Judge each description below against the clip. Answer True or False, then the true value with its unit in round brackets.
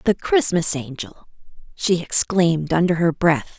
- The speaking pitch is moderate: True (170 Hz)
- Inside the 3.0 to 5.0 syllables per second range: True (4.5 syllables/s)